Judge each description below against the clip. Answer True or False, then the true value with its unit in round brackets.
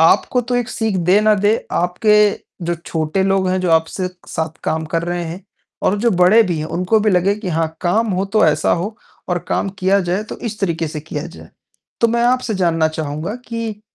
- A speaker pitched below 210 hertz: True (185 Hz)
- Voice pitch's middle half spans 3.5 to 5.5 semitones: True (4.4 semitones)